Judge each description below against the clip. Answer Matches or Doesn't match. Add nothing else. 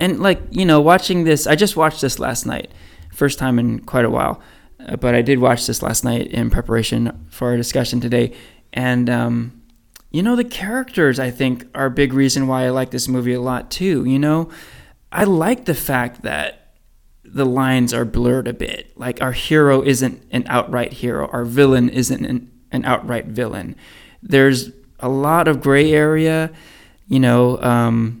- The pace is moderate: Matches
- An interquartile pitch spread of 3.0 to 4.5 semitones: Matches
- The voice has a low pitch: Matches